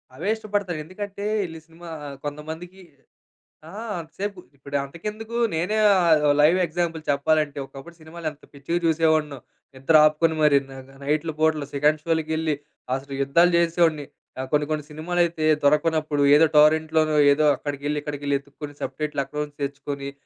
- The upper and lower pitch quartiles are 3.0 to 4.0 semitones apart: No, narrow, 2.5 semitones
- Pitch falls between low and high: Yes, medium, 155 Hz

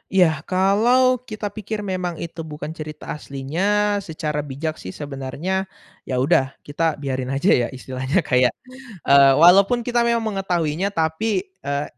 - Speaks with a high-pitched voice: No, medium, 160 Hz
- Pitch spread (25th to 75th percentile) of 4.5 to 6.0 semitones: Yes, wide, 5.4 semitones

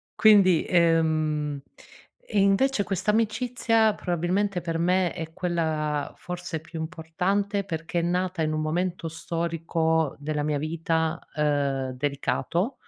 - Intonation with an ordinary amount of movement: Yes, average, 3.0 semitones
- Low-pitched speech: No, medium, 165 Hz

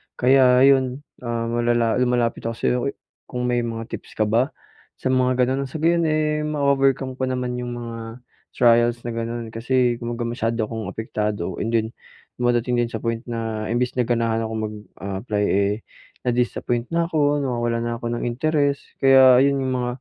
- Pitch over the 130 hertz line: No, low, 120 Hz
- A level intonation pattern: Yes, narrow, 2.1 semitones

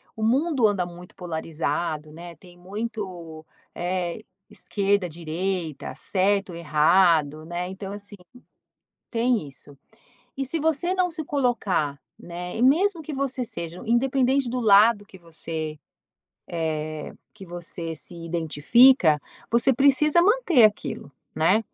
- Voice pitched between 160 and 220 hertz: Yes, high, 190 Hz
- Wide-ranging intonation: Yes, wide, 6.9 semitones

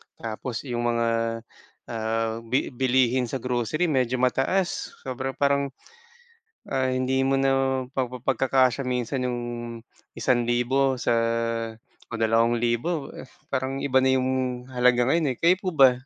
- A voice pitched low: Yes, low, 130 Hz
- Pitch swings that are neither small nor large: No, narrow, 2.1 semitones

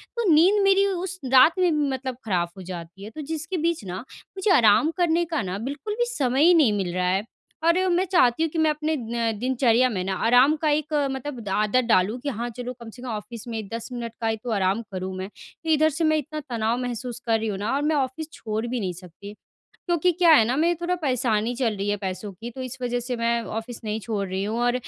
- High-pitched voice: Yes, high, 245 Hz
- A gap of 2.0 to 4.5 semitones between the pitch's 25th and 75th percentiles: No, wide, 6.4 semitones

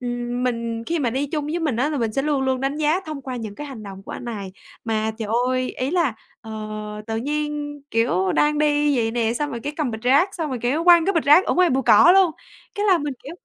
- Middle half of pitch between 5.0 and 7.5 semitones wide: No, average, 4.3 semitones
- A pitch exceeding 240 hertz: Yes, very high, 270 Hz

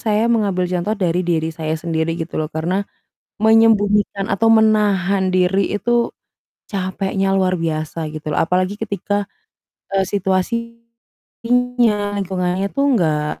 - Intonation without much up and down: No, average, 3.5 semitones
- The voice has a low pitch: No, high, 195 Hz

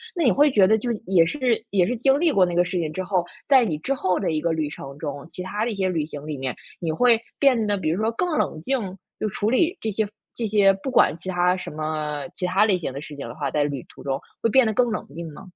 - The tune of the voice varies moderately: No, wide, 6.4 semitones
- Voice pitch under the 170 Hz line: No, medium, 185 Hz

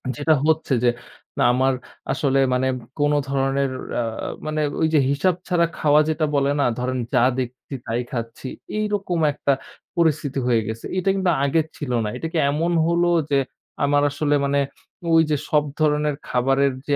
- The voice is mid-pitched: Yes, medium, 145 Hz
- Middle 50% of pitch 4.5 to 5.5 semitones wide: No, average, 3.0 semitones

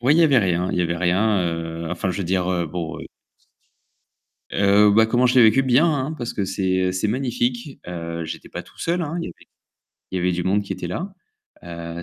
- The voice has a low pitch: Yes, very low, 95 Hz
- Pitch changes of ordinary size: No, wide, 5.7 semitones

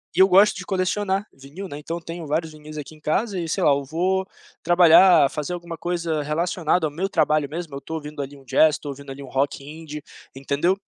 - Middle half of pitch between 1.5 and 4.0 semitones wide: Yes, average, 3.4 semitones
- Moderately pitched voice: Yes, medium, 160 Hz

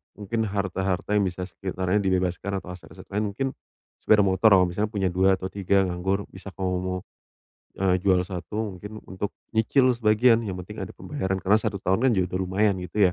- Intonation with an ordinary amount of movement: No, narrow, 2.0 semitones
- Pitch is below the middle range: Yes, very low, 95 Hz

